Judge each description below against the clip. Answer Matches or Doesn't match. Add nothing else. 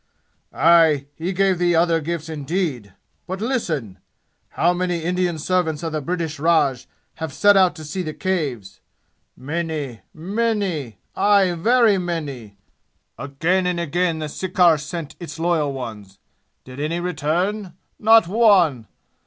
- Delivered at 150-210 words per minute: Doesn't match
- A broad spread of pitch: Doesn't match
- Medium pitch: Matches